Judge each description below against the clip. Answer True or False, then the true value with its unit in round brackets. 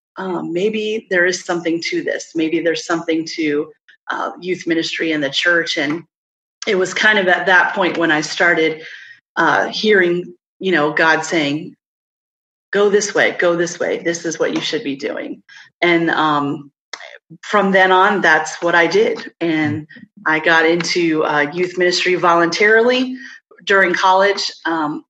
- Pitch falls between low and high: True (175 Hz)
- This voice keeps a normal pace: True (160 wpm)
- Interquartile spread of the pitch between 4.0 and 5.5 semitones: False (3.2 semitones)